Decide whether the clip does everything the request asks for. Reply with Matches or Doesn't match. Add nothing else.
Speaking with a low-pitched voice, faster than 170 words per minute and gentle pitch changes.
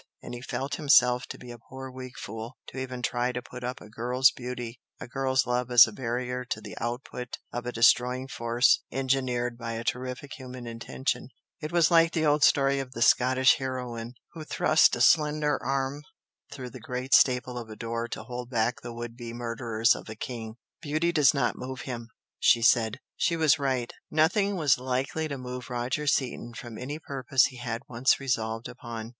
Matches